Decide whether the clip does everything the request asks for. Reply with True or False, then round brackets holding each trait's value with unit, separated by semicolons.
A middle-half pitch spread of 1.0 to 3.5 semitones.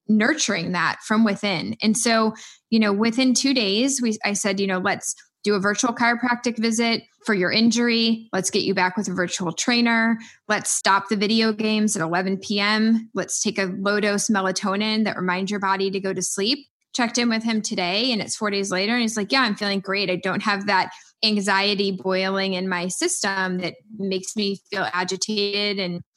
True (2.8 semitones)